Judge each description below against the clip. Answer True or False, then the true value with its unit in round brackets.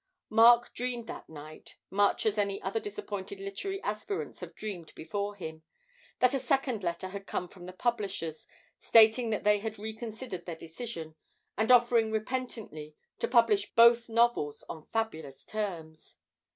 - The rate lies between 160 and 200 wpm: False (145 wpm)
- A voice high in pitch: True (210 Hz)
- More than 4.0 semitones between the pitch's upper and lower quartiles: True (4.5 semitones)